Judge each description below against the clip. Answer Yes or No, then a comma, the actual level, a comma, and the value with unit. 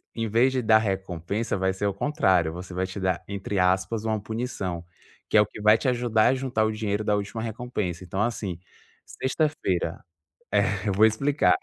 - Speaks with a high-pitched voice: No, low, 105 Hz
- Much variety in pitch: No, average, 3.4 semitones